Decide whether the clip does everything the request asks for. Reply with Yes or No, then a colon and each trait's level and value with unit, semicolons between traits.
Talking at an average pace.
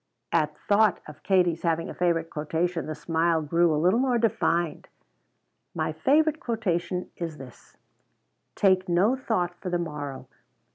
Yes: average, 145 wpm